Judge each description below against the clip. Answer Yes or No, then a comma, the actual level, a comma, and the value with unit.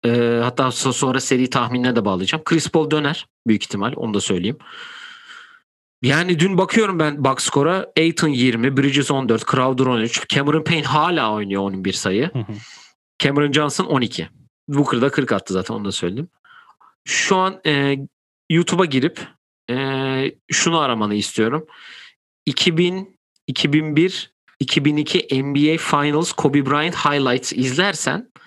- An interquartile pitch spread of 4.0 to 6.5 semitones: Yes, average, 4.6 semitones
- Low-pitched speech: No, medium, 145 Hz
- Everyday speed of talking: Yes, average, 130 wpm